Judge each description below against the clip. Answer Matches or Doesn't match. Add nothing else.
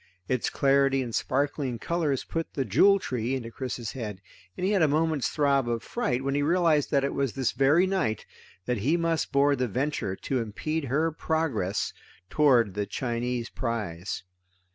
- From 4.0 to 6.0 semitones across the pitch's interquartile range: Matches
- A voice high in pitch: Doesn't match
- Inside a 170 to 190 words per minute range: Matches